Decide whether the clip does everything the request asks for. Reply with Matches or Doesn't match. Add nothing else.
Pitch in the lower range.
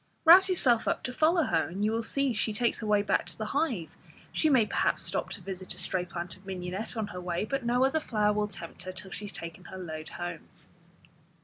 Doesn't match